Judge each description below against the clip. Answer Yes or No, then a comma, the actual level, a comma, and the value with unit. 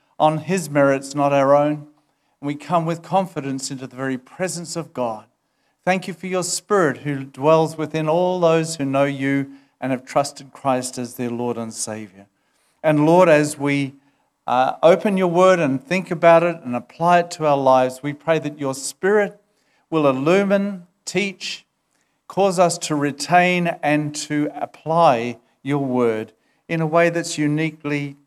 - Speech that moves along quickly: No, average, 170 wpm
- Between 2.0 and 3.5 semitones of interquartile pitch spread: No, average, 4.0 semitones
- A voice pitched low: No, medium, 150 Hz